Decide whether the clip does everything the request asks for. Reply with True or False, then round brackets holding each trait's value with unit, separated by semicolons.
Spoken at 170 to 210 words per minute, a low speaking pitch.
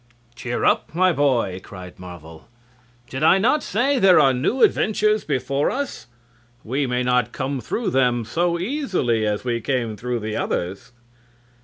False (155 wpm; 130 Hz)